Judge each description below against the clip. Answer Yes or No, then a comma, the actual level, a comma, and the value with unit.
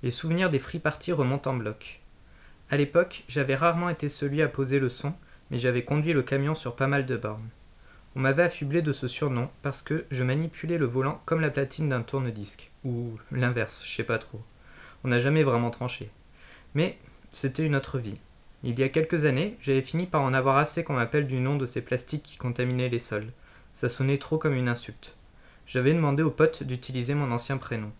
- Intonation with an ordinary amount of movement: Yes, average, 3.4 semitones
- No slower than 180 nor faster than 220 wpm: Yes, average, 210 wpm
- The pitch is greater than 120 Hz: Yes, low, 135 Hz